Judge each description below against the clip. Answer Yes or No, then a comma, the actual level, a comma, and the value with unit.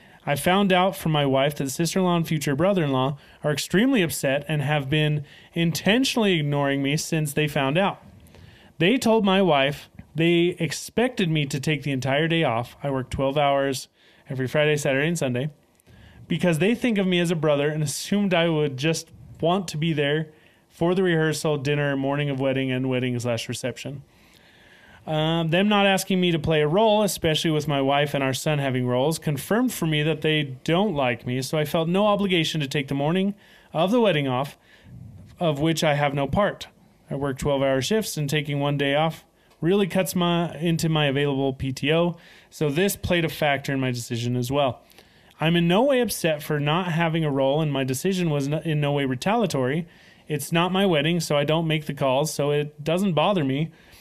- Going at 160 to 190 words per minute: No, average, 200 wpm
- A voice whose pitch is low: No, medium, 155 Hz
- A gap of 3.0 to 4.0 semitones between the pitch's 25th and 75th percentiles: Yes, average, 3.7 semitones